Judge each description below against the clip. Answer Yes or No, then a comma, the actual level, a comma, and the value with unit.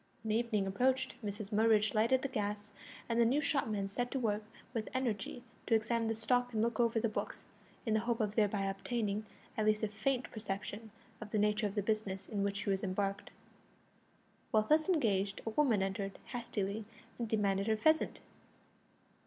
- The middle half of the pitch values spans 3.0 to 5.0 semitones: No, narrow, 2.4 semitones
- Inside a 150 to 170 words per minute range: No, average, 185 wpm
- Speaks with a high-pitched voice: Yes, high, 215 Hz